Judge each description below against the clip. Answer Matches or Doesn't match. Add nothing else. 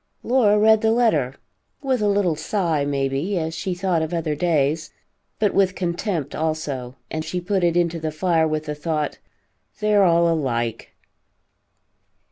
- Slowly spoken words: Doesn't match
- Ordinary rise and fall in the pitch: Matches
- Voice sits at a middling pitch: Matches